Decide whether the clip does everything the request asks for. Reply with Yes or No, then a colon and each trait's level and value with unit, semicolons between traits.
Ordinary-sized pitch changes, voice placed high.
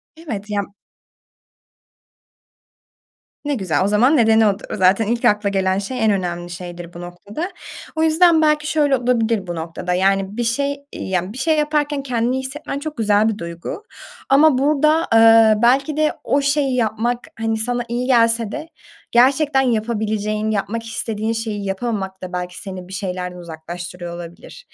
No: wide, 5.8 semitones; high, 225 Hz